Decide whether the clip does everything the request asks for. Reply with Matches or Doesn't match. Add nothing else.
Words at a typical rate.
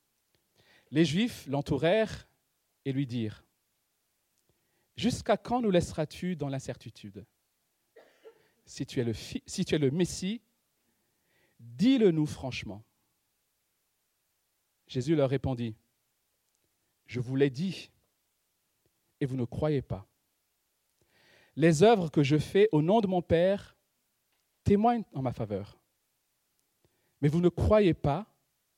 Doesn't match